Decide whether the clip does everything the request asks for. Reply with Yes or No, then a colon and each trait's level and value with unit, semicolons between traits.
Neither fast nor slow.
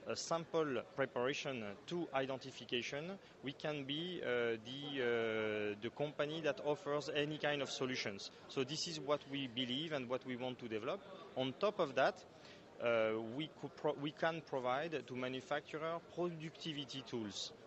Yes: average, 155 wpm